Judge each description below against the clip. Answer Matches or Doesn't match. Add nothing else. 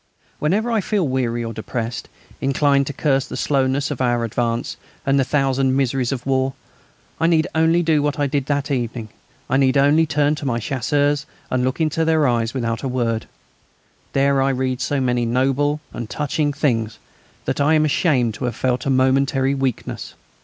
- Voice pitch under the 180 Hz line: Matches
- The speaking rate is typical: Matches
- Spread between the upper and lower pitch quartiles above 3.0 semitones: Doesn't match